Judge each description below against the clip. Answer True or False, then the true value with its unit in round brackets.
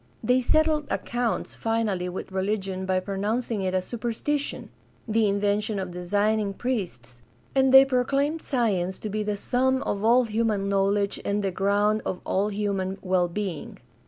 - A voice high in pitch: True (205 Hz)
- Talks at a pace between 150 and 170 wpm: True (160 wpm)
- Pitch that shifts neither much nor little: True (3.7 semitones)